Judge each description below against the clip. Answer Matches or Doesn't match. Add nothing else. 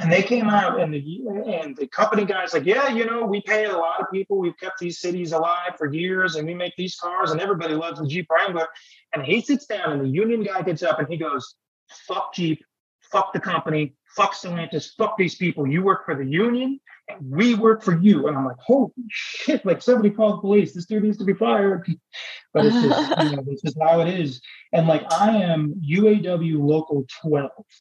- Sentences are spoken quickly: Matches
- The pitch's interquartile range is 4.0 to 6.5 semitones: Matches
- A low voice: Doesn't match